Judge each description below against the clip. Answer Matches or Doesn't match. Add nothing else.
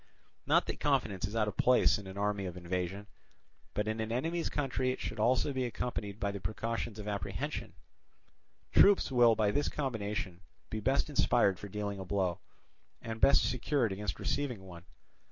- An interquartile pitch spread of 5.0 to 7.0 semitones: Doesn't match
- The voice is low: Matches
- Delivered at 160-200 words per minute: Matches